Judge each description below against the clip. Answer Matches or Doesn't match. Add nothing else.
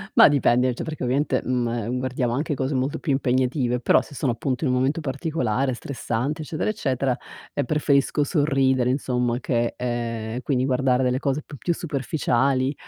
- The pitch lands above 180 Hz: Doesn't match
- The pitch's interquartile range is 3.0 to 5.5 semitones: Doesn't match